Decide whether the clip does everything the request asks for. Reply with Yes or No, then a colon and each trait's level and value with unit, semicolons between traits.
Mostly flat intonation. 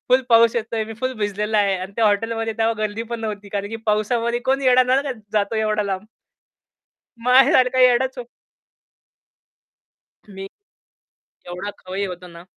No: average, 3.1 semitones